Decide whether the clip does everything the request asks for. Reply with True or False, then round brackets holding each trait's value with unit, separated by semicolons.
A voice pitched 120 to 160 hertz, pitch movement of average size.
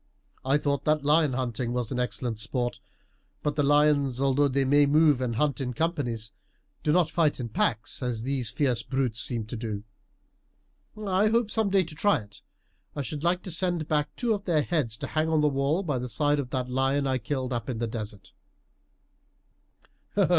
True (140 Hz; 4.0 semitones)